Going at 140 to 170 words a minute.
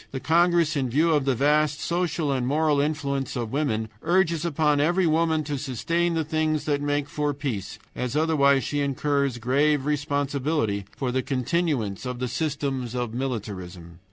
Yes: average, 165 wpm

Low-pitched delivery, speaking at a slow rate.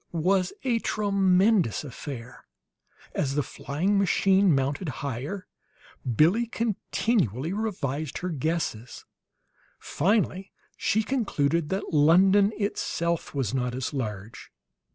No: medium, 170 Hz; slow, 105 wpm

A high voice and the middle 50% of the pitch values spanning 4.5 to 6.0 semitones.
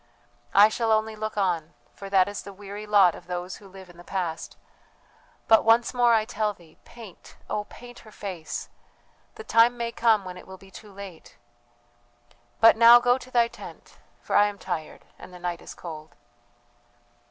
No: high, 205 Hz; average, 3.8 semitones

